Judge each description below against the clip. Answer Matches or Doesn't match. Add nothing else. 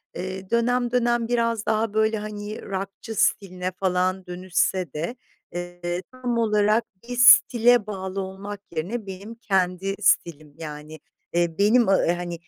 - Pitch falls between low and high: Doesn't match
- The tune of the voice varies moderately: Matches